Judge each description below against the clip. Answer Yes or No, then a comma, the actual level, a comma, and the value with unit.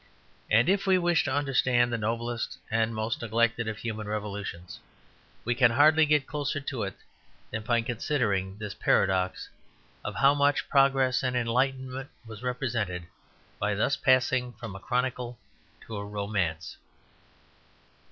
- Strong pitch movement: No, average, 3.8 semitones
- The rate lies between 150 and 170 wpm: No, average, 140 wpm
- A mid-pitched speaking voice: No, low, 120 Hz